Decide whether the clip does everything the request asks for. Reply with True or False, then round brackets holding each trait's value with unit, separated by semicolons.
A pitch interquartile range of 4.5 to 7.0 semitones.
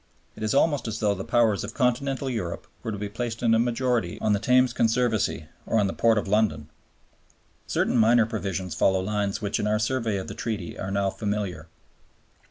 False (3.0 semitones)